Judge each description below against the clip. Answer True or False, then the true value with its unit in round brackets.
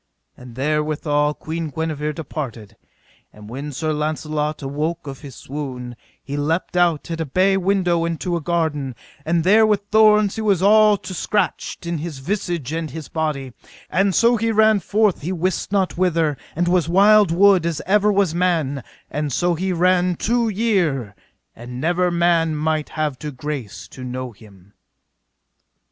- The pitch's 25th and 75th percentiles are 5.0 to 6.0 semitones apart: False (4.1 semitones)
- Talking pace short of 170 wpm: True (160 wpm)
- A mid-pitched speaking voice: True (165 Hz)